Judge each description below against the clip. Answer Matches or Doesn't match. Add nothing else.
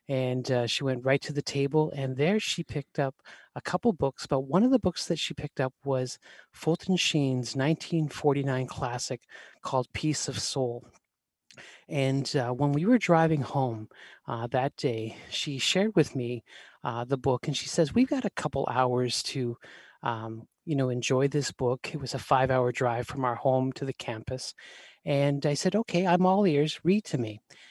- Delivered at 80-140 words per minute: Doesn't match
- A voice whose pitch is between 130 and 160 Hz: Matches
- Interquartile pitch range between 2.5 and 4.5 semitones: Matches